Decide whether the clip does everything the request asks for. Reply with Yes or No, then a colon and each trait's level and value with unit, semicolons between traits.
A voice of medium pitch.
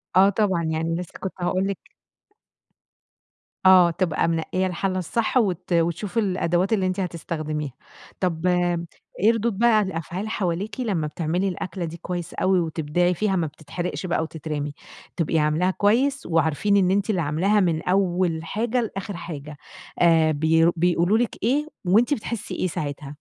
Yes: medium, 180 Hz